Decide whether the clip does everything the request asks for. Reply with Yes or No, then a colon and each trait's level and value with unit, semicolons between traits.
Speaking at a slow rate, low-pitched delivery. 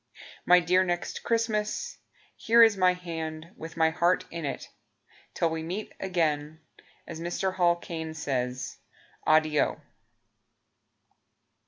No: slow, 120 wpm; medium, 170 Hz